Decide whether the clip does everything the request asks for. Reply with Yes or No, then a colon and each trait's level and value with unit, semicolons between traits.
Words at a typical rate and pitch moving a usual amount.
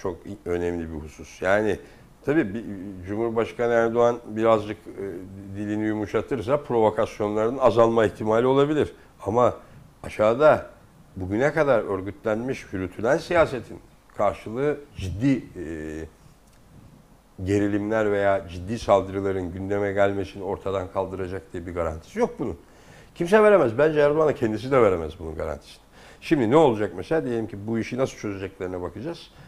Yes: average, 120 wpm; average, 3.8 semitones